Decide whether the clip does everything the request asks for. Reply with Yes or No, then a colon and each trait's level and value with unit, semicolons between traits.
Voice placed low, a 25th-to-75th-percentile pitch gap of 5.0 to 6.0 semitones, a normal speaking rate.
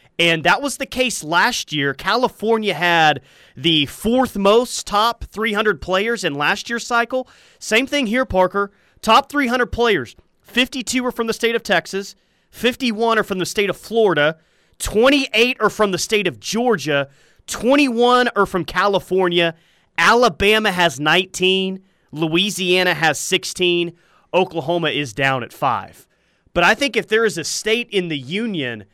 No: high, 200 Hz; average, 5.3 semitones; average, 150 wpm